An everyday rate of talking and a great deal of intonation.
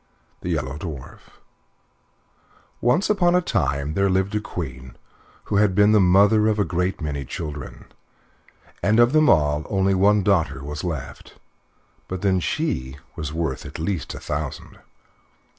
Yes: average, 150 wpm; wide, 5.7 semitones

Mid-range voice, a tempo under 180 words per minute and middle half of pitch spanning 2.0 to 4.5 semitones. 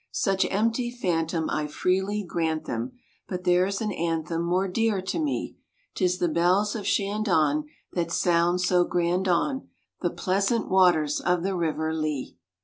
Yes: medium, 180 Hz; average, 150 wpm; average, 3.0 semitones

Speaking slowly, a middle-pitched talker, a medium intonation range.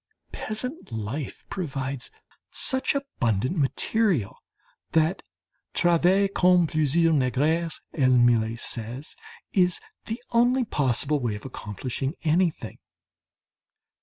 No: slow, 95 wpm; medium, 155 Hz; wide, 6.3 semitones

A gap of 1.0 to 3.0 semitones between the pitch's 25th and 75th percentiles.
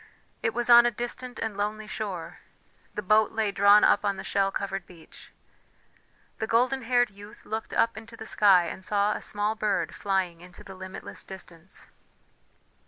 Yes: narrow, 2.5 semitones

